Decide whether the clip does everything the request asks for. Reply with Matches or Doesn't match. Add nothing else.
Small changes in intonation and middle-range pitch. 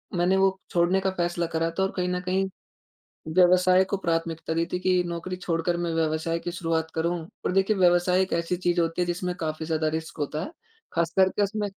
Matches